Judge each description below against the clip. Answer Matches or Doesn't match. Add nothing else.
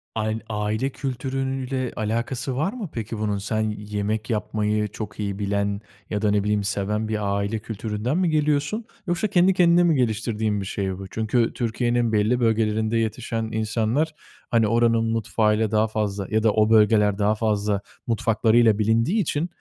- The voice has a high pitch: Doesn't match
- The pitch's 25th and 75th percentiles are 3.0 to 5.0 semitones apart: Doesn't match